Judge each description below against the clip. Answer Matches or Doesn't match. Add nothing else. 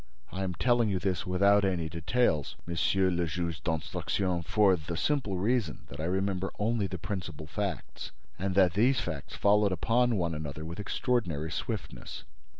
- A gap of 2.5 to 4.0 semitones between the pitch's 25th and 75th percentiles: Matches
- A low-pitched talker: Matches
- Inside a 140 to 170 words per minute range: Matches